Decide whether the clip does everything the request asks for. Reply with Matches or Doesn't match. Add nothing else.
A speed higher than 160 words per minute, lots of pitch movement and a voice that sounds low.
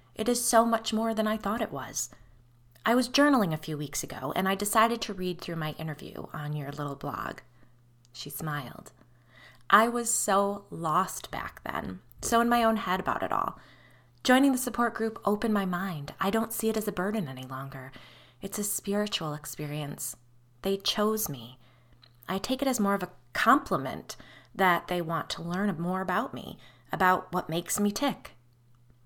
Doesn't match